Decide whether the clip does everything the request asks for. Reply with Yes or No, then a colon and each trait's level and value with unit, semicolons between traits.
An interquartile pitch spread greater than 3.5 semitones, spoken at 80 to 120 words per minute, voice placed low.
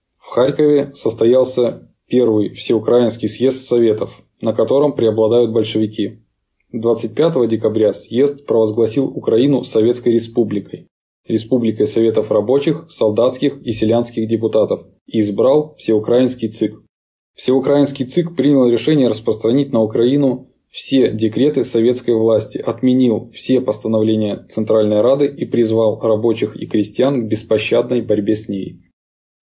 No: average, 2.7 semitones; slow, 110 wpm; low, 115 Hz